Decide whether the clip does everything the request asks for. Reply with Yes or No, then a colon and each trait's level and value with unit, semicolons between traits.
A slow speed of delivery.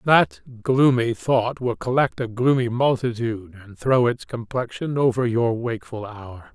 No: average, 145 wpm